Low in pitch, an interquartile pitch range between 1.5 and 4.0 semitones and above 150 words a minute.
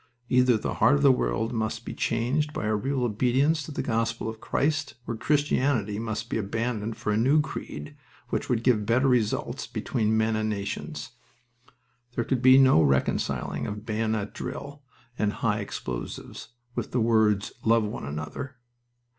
Yes: low, 115 Hz; average, 3.3 semitones; average, 165 wpm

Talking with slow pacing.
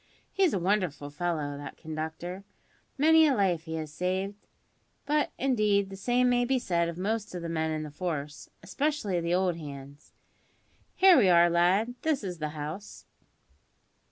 No: average, 165 wpm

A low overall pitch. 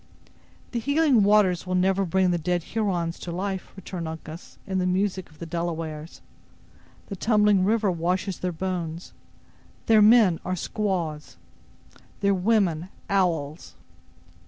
No: medium, 185 Hz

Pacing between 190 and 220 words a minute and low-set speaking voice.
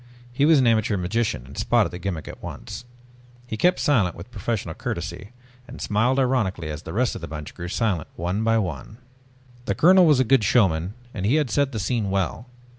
Yes: fast, 205 wpm; low, 105 Hz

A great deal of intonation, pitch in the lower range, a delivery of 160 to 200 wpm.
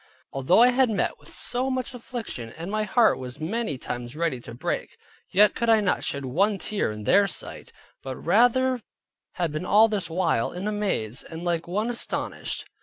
No: wide, 7.3 semitones; high, 195 Hz; average, 190 wpm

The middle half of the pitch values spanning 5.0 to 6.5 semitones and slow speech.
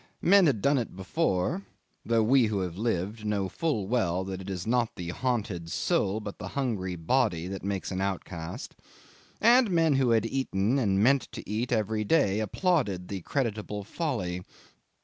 No: wide, 5.4 semitones; average, 175 wpm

